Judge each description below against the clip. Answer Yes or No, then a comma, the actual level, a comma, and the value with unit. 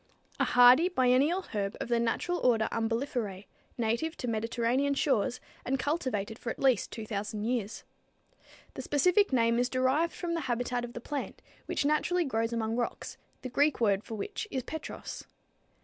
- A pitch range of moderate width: Yes, average, 3.8 semitones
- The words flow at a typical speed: Yes, average, 165 wpm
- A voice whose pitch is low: No, high, 245 Hz